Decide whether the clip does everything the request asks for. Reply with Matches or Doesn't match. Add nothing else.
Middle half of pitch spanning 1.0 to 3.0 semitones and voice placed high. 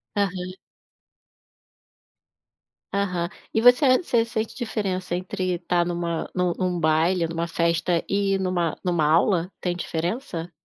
Doesn't match